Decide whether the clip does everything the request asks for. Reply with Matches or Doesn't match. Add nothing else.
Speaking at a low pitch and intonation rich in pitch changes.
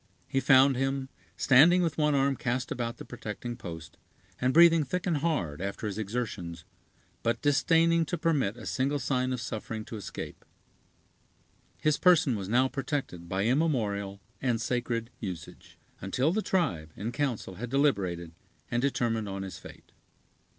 Matches